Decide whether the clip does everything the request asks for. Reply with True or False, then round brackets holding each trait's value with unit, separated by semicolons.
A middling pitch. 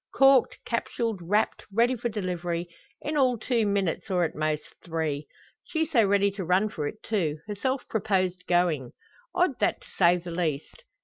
False (195 Hz)